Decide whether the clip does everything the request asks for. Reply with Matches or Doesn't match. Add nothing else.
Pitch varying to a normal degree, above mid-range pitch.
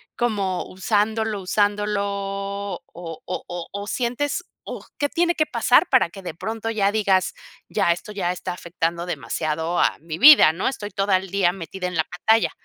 Matches